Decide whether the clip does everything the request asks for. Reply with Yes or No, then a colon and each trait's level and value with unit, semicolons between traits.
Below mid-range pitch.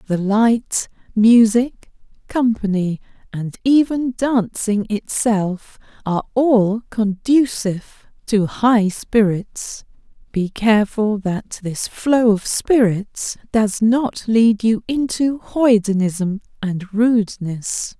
No: high, 220 Hz